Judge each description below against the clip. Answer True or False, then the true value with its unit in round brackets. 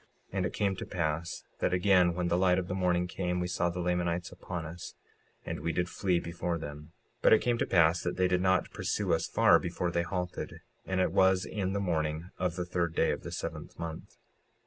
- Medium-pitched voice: False (90 Hz)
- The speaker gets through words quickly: True (235 wpm)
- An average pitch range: False (1.4 semitones)